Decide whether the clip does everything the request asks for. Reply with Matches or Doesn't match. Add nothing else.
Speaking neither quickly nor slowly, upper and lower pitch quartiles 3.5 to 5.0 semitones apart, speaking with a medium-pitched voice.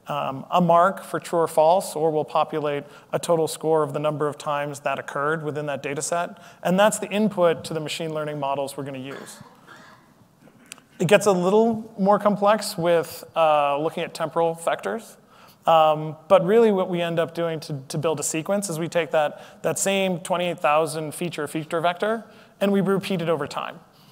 Matches